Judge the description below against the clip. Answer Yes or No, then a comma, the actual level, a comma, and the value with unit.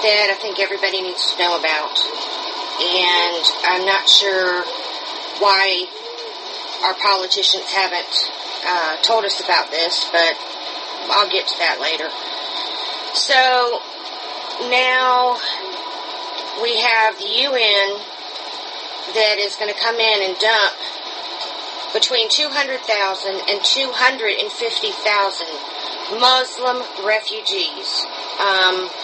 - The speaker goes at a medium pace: No, slow, 100 wpm